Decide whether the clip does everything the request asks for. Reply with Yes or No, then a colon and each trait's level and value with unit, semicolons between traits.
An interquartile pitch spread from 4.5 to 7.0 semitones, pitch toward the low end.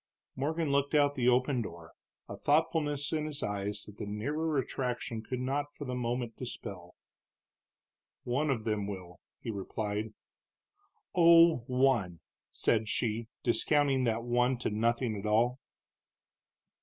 Yes: average, 4.9 semitones; low, 125 Hz